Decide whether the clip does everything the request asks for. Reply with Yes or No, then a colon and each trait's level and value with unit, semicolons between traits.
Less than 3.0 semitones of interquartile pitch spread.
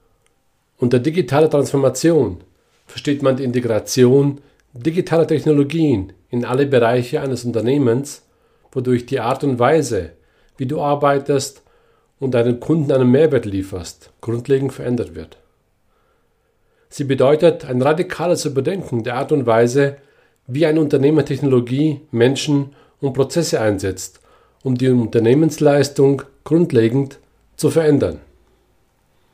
No: average, 3.3 semitones